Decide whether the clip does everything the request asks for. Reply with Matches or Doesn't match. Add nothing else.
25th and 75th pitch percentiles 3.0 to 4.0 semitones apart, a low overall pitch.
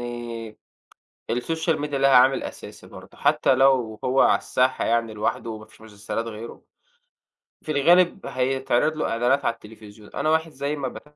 Matches